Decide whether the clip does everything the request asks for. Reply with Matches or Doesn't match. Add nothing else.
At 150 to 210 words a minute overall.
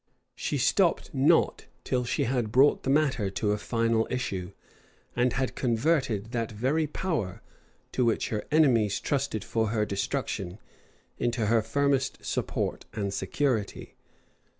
Doesn't match